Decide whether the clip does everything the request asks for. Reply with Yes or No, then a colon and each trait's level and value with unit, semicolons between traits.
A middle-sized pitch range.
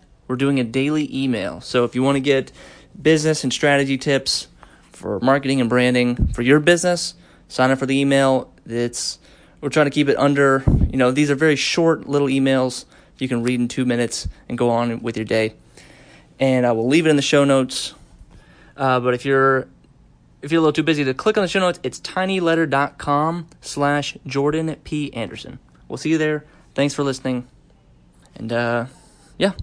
Yes: average, 3.2 semitones